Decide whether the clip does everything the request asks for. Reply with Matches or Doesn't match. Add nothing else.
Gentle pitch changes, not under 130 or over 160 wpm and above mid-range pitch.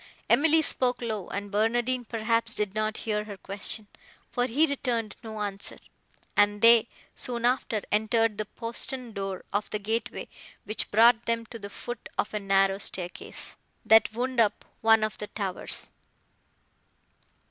Matches